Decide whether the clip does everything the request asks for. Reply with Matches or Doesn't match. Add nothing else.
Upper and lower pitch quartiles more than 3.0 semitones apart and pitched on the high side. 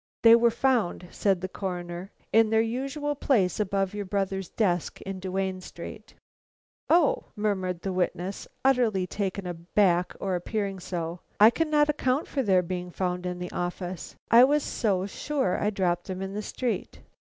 Matches